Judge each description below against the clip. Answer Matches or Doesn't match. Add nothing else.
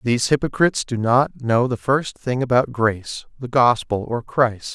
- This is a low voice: Matches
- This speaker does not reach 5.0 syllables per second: Matches